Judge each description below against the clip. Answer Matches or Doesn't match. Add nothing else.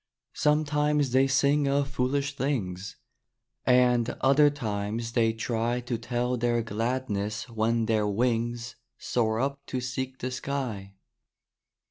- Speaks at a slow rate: Matches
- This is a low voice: Matches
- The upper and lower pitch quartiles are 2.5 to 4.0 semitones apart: Matches